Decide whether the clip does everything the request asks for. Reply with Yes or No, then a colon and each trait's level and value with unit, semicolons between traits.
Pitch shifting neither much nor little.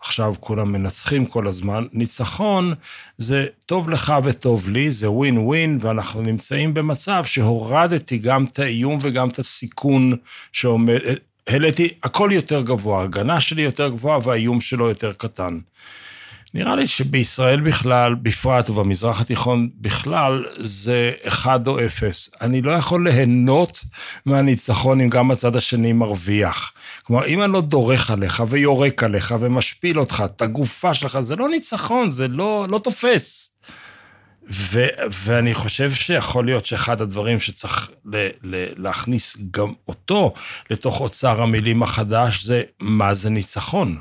Yes: average, 3.9 semitones